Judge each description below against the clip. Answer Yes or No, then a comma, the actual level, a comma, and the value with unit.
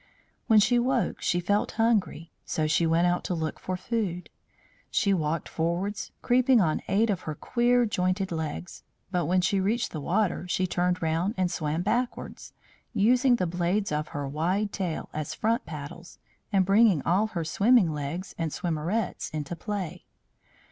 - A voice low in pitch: No, medium, 180 Hz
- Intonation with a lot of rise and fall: No, average, 4.3 semitones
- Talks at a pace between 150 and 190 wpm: Yes, average, 165 wpm